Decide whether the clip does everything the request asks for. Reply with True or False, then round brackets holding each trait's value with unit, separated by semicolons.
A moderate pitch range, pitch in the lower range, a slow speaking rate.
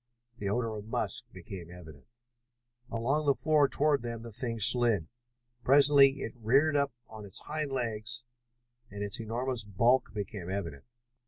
False (4.8 semitones; 115 Hz; 150 wpm)